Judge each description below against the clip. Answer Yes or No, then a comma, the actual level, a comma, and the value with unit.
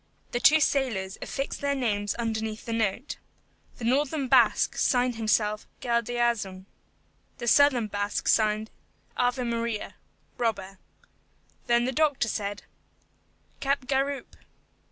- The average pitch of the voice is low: No, high, 235 Hz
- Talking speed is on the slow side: Yes, slow, 110 wpm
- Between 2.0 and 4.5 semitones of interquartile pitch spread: Yes, average, 3.5 semitones